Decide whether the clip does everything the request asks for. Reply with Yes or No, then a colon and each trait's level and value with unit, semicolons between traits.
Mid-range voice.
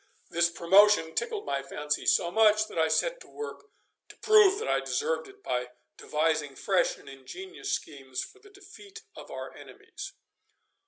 No: high, 215 Hz